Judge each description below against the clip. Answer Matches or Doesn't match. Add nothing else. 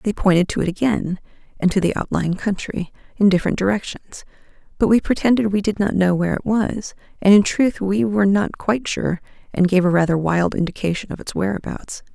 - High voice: Matches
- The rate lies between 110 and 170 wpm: Doesn't match